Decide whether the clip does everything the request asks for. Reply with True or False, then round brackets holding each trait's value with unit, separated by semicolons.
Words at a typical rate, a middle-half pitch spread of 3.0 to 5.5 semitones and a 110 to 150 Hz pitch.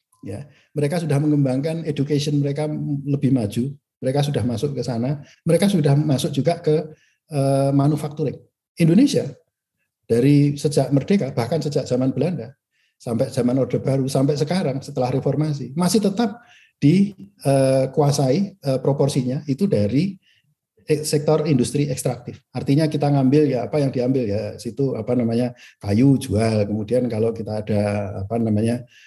True (130 wpm; 3.5 semitones; 140 Hz)